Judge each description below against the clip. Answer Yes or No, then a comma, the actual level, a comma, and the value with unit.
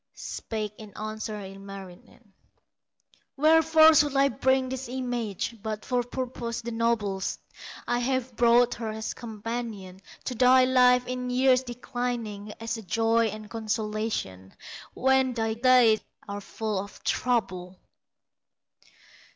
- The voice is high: Yes, high, 230 Hz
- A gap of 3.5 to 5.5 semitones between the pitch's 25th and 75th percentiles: No, average, 2.9 semitones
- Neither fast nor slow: No, slow, 120 wpm